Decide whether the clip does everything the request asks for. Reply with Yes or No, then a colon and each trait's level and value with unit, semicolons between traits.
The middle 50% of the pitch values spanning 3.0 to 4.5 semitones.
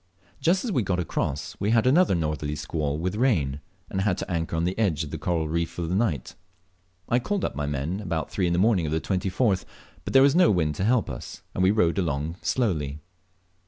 No: wide, 5.6 semitones